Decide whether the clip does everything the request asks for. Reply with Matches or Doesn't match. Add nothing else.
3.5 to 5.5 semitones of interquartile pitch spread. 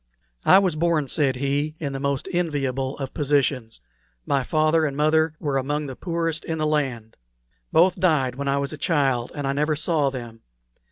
Doesn't match